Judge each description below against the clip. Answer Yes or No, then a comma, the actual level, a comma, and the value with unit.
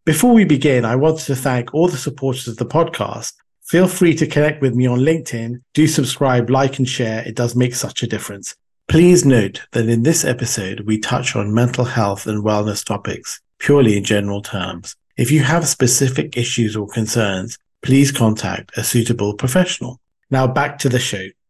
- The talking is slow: No, average, 185 wpm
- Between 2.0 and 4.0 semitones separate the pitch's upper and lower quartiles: No, average, 4.6 semitones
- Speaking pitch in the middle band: No, low, 125 Hz